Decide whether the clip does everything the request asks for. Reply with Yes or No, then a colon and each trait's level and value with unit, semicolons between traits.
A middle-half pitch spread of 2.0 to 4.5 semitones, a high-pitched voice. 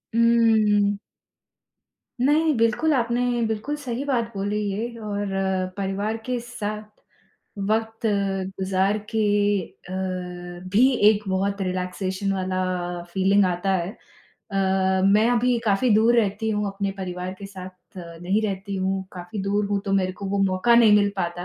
Yes: average, 2.8 semitones; high, 200 Hz